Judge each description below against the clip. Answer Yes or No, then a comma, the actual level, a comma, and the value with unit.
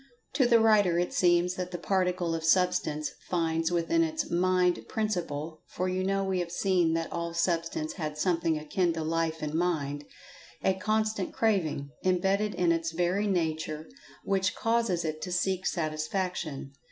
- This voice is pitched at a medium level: Yes, medium, 175 Hz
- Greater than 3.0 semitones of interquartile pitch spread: No, average, 2.7 semitones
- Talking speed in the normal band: Yes, average, 160 wpm